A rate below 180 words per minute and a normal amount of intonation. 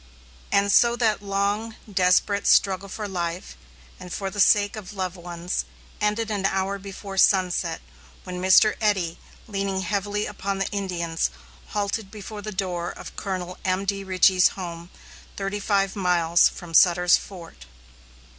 No: average, 140 wpm; narrow, 2.1 semitones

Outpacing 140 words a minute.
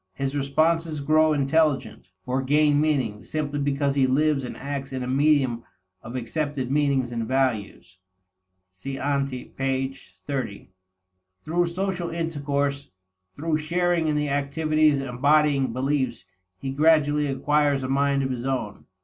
No: slow, 135 wpm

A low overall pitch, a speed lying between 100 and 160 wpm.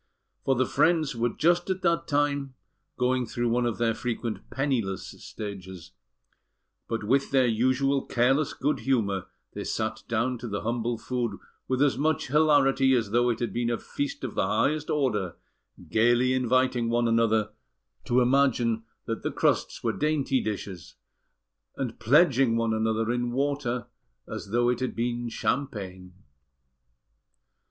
Yes: low, 120 Hz; average, 150 wpm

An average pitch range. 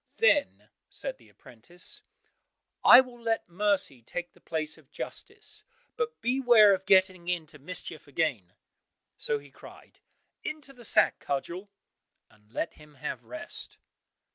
No: wide, 8.2 semitones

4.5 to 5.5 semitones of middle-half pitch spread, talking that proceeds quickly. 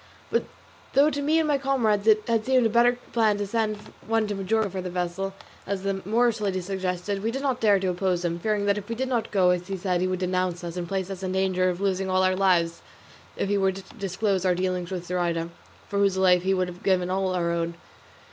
No: average, 2.8 semitones; fast, 245 wpm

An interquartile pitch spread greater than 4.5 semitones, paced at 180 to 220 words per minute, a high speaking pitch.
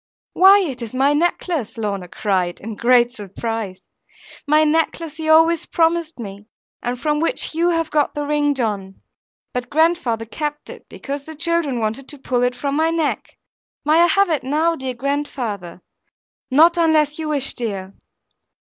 No: wide, 5.6 semitones; average, 165 wpm; very high, 285 Hz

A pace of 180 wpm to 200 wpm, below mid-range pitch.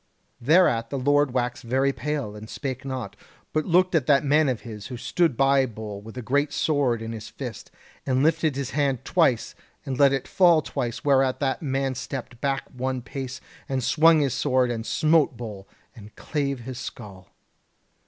Yes: average, 185 wpm; low, 130 Hz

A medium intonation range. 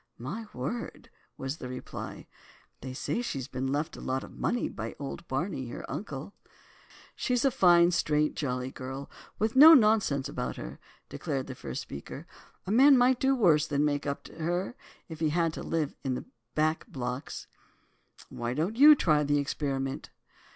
No: wide, 7.1 semitones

